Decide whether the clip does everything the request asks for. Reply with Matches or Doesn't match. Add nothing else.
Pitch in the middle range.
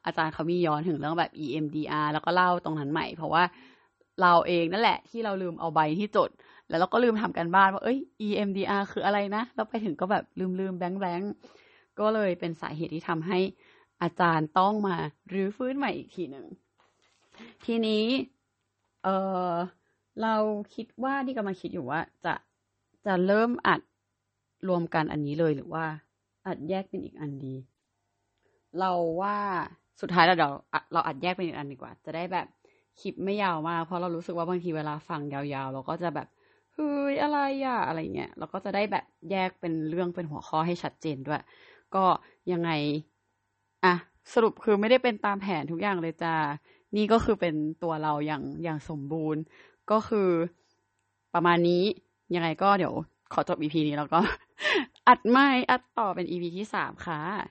Matches